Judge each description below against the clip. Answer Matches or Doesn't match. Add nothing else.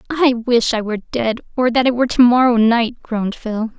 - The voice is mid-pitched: Doesn't match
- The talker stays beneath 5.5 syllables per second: Matches